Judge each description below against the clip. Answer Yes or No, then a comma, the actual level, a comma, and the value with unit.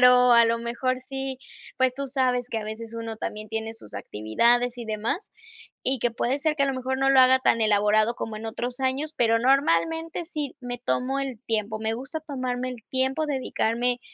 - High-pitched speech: Yes, very high, 250 Hz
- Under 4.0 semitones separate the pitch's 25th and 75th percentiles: Yes, average, 2.9 semitones